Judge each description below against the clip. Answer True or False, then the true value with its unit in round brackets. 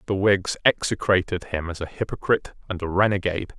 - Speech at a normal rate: True (165 wpm)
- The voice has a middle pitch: False (95 Hz)